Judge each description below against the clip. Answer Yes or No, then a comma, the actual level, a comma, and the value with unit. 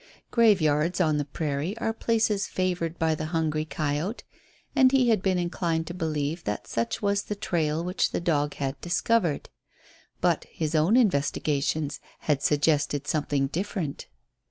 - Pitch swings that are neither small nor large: Yes, average, 4.3 semitones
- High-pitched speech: No, medium, 160 Hz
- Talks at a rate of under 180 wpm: Yes, average, 150 wpm